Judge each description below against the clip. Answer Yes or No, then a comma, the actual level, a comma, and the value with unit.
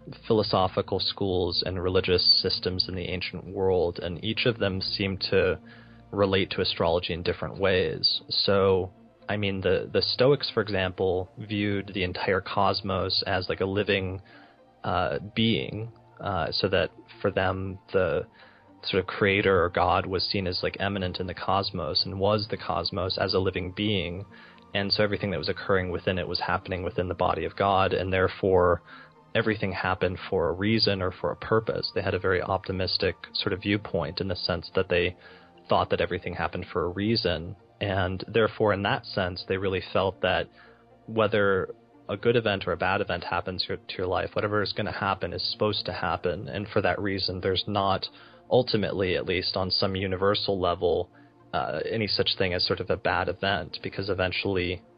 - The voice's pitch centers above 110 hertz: No, low, 100 Hz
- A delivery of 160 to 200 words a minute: Yes, average, 180 wpm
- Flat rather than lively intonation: Yes, narrow, 2.3 semitones